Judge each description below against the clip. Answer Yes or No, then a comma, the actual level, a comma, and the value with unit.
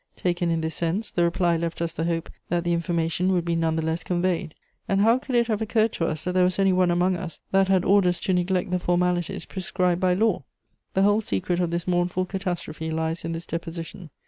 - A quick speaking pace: Yes, fast, 230 wpm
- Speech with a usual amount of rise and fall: No, narrow, 2.0 semitones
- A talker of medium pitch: Yes, medium, 175 Hz